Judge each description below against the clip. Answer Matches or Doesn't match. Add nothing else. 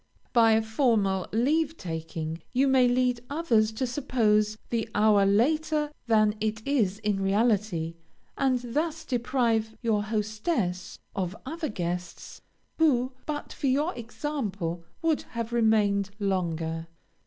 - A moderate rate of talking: Doesn't match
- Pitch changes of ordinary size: Matches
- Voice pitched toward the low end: Doesn't match